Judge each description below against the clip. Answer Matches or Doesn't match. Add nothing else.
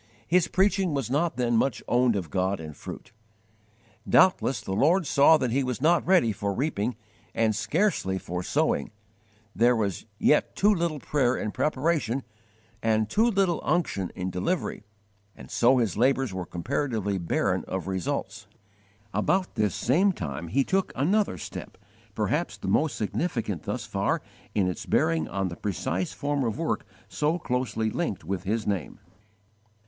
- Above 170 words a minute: Doesn't match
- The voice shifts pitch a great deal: Matches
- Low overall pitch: Matches